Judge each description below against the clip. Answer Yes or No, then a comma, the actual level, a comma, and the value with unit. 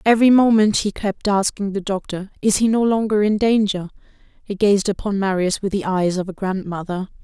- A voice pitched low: No, high, 200 Hz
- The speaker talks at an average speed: Yes, average, 190 wpm